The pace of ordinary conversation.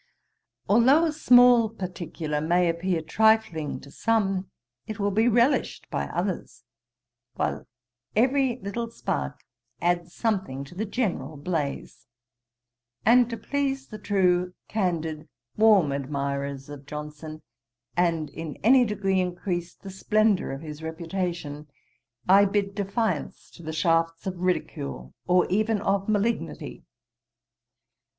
No: slow, 120 wpm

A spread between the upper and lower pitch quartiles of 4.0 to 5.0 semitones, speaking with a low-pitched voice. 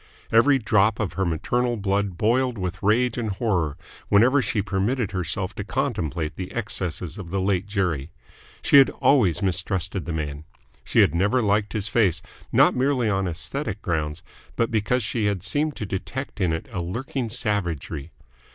Yes: average, 4.6 semitones; low, 100 Hz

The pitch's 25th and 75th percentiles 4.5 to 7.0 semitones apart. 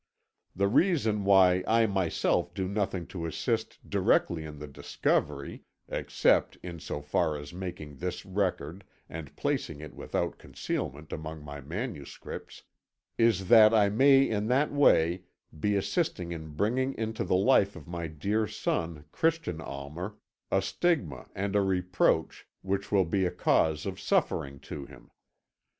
Yes: average, 5.2 semitones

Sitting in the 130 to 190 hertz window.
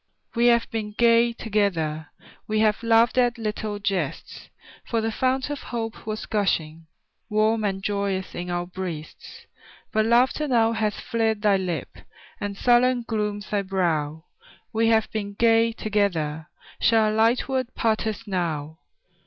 No: high, 215 Hz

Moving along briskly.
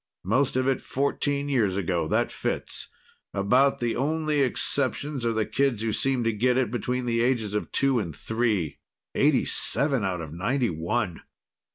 No: average, 170 wpm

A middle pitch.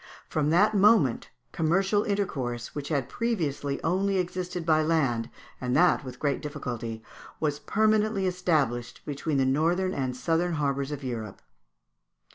Yes: medium, 155 Hz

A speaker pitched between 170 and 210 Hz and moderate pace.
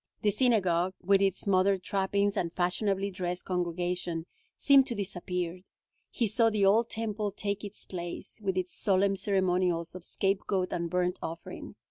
Yes: high, 190 Hz; average, 150 wpm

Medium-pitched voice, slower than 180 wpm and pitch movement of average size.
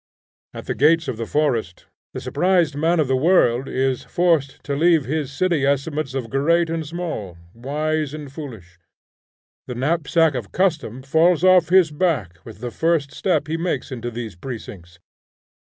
Yes: medium, 145 Hz; average, 165 wpm; average, 4.8 semitones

